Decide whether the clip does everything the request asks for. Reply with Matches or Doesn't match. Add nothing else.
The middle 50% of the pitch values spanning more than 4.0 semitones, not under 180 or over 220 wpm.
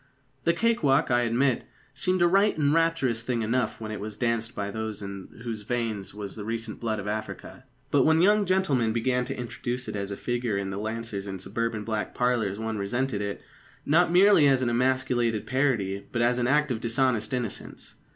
Doesn't match